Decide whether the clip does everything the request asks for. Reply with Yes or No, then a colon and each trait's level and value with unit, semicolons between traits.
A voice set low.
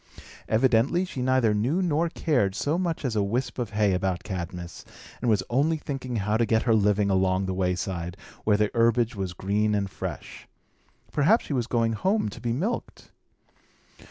Yes: low, 110 Hz